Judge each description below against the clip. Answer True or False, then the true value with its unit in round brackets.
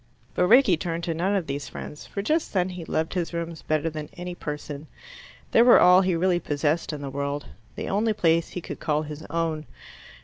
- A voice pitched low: False (165 Hz)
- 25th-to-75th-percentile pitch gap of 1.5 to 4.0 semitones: True (3.1 semitones)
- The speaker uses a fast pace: True (210 wpm)